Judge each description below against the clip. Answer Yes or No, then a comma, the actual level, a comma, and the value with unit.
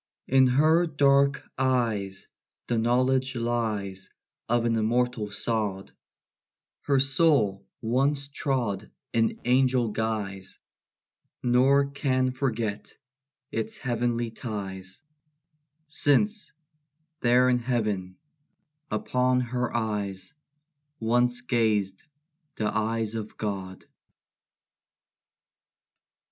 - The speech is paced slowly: Yes, slow, 85 wpm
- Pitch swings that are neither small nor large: Yes, average, 3.5 semitones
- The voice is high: No, low, 120 Hz